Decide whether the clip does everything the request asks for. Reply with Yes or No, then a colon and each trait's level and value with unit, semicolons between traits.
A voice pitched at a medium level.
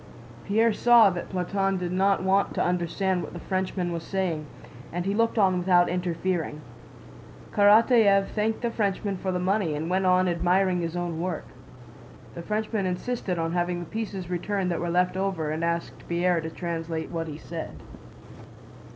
Yes: medium, 180 Hz